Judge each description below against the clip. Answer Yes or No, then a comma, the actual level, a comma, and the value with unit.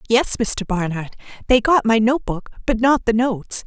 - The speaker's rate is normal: Yes, average, 195 wpm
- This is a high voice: Yes, high, 225 Hz